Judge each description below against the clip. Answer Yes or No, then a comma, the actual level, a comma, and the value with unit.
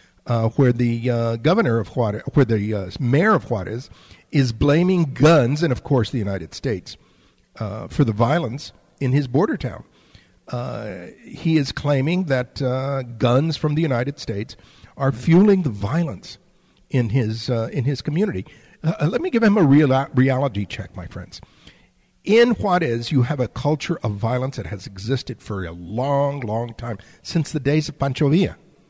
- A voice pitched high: No, low, 135 Hz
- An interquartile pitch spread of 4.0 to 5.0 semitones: Yes, average, 4.6 semitones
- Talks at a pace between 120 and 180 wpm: Yes, average, 175 wpm